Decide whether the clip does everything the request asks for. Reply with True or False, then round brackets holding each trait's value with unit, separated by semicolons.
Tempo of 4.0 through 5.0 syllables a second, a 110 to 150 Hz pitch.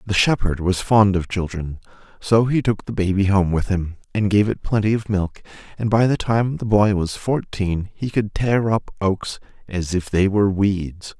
False (4.5 syllables/s; 100 Hz)